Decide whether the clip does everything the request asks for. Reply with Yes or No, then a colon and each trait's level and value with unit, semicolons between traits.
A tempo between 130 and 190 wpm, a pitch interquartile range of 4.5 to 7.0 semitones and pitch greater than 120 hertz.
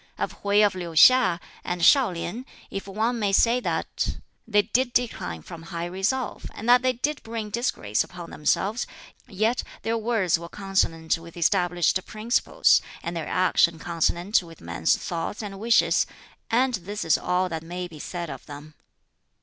Yes: average, 165 wpm; average, 5.1 semitones; high, 190 Hz